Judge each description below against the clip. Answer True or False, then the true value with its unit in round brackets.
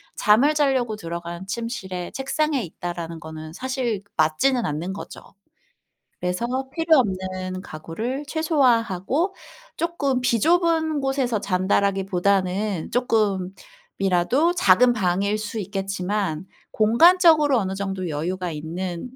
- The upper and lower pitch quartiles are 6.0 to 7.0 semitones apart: True (6.5 semitones)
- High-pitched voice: True (205 Hz)